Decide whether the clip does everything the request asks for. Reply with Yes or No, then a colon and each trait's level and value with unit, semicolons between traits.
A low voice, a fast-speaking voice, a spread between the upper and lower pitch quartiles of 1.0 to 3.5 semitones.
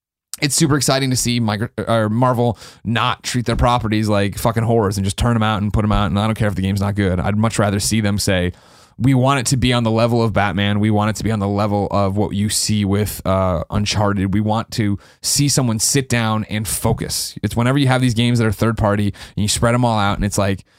Yes: low, 110 Hz; fast, 260 wpm; average, 2.8 semitones